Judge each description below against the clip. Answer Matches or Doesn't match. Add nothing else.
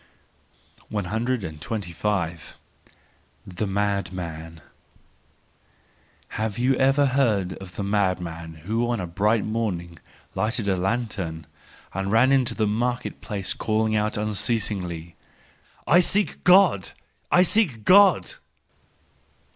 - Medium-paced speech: Doesn't match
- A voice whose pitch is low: Matches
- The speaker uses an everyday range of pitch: Matches